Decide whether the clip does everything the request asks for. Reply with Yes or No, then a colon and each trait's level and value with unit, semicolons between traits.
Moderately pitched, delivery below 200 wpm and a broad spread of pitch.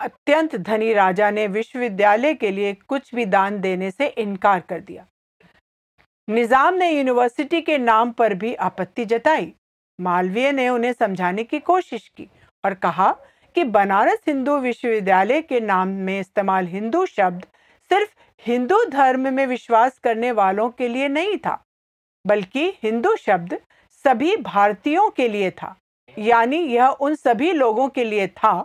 No: high, 235 Hz; average, 145 wpm; wide, 5.8 semitones